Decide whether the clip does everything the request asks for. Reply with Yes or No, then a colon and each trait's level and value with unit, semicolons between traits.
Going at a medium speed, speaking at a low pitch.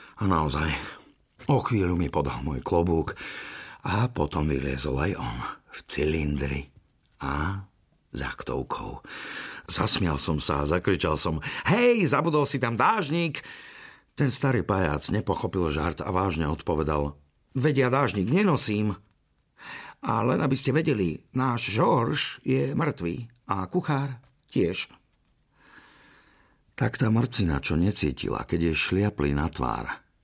Yes: average, 120 wpm; very low, 95 Hz